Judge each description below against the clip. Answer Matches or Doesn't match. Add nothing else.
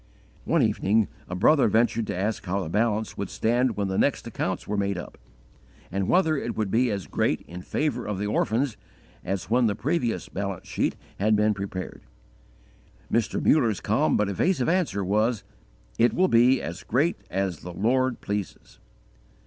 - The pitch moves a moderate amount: Matches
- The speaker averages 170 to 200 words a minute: Matches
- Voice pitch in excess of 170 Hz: Doesn't match